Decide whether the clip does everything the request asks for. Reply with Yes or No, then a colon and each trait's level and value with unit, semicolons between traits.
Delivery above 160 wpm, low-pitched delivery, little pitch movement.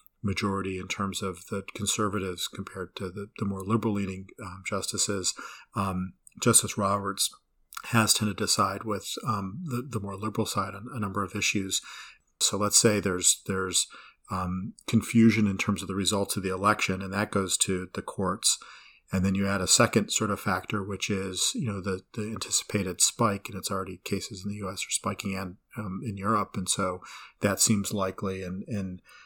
Yes: average, 190 wpm; low, 100 Hz; narrow, 1.9 semitones